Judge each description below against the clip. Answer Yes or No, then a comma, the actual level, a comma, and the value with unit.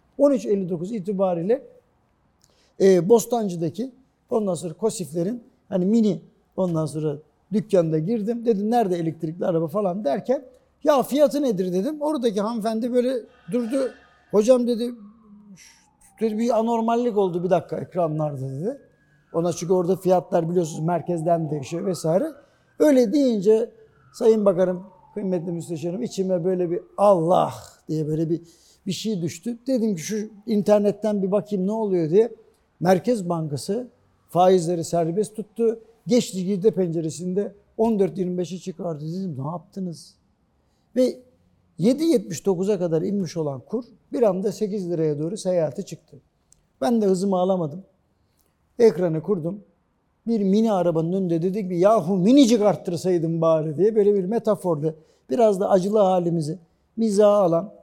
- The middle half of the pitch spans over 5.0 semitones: No, average, 4.4 semitones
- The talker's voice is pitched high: Yes, high, 195 Hz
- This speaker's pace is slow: No, average, 125 wpm